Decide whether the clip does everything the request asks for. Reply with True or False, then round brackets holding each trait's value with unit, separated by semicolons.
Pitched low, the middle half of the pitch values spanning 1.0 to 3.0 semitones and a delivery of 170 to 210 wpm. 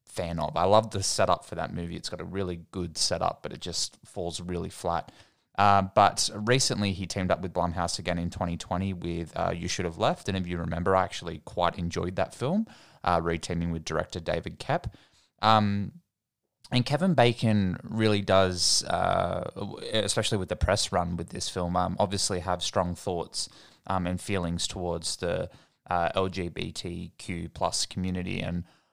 True (90 Hz; 2.7 semitones; 175 wpm)